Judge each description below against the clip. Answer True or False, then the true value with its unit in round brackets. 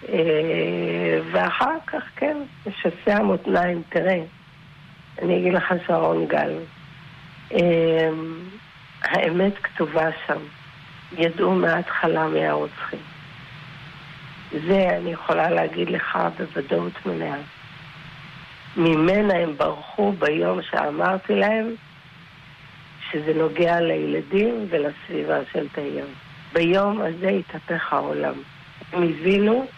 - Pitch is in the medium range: True (160 Hz)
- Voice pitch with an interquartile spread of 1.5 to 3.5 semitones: True (3.2 semitones)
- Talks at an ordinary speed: False (90 wpm)